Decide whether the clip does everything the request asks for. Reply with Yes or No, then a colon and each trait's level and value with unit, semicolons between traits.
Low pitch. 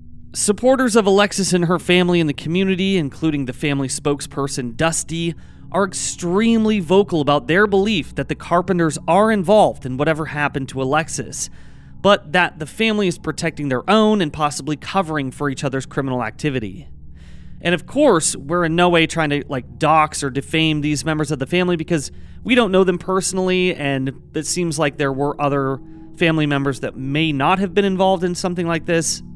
No: medium, 160 Hz